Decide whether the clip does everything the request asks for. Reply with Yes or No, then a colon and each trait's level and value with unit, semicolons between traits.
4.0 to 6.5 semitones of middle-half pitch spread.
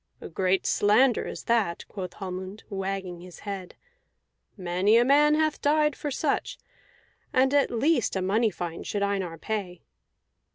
Yes: wide, 5.5 semitones